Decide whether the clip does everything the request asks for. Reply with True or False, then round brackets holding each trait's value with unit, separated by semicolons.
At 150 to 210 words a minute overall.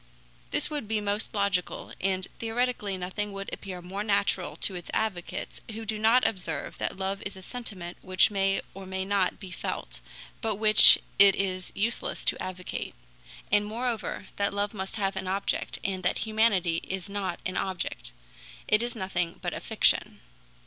True (170 wpm)